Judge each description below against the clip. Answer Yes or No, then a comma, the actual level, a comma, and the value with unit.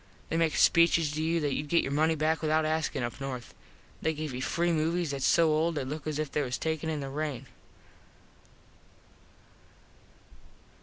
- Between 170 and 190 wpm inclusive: Yes, average, 185 wpm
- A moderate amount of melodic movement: No, narrow, 2.1 semitones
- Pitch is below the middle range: No, medium, 155 Hz